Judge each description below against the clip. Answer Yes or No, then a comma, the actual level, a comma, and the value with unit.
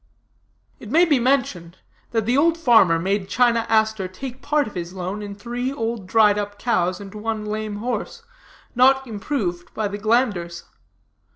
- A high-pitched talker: Yes, high, 220 Hz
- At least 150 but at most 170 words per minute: Yes, average, 165 wpm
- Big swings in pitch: No, average, 3.9 semitones